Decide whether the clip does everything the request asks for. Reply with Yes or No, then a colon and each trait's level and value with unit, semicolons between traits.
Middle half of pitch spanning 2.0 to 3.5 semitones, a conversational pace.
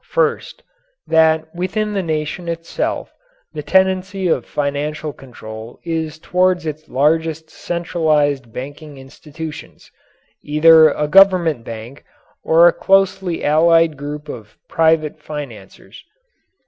No: average, 2.7 semitones; slow, 110 wpm